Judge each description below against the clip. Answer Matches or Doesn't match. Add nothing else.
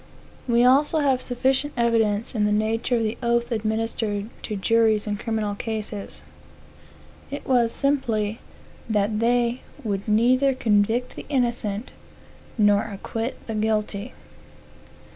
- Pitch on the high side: Matches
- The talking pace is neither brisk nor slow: Doesn't match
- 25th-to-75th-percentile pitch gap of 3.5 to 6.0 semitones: Doesn't match